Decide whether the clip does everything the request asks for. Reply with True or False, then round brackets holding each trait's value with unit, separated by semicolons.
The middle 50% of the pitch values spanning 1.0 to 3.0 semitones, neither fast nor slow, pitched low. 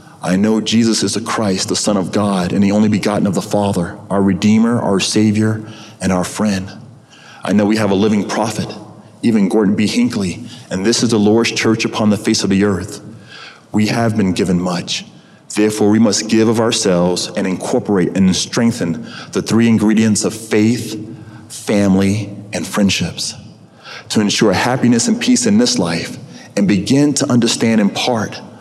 True (2.4 semitones; 175 wpm; 110 Hz)